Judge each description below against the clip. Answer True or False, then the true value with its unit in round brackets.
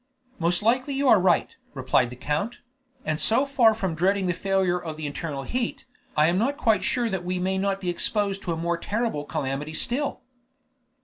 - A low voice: False (185 Hz)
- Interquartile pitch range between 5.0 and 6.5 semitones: True (5.5 semitones)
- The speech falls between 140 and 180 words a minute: False (195 wpm)